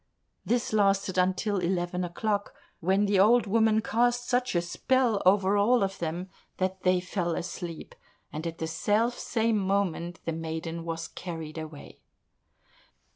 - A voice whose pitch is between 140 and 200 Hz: Yes, high, 190 Hz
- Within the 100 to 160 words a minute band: Yes, average, 145 wpm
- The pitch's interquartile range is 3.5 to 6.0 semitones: Yes, average, 3.9 semitones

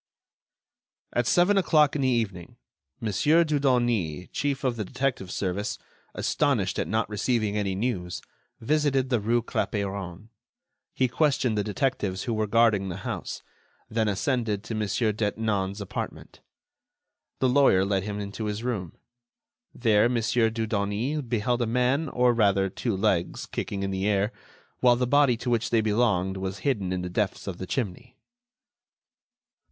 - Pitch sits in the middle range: No, low, 110 Hz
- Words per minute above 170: No, average, 150 wpm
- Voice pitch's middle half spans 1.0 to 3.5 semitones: No, average, 3.9 semitones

